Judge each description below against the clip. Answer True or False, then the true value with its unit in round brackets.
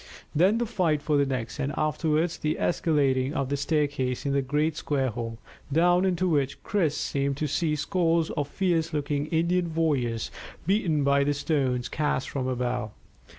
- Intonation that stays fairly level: False (3.1 semitones)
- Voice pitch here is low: False (150 Hz)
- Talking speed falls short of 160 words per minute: False (170 wpm)